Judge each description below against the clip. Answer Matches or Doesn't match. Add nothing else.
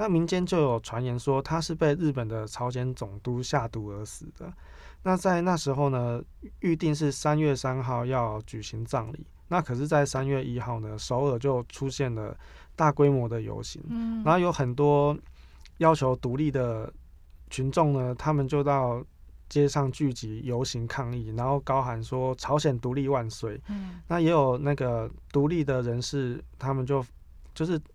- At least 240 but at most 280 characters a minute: Matches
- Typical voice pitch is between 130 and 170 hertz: Matches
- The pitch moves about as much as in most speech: Matches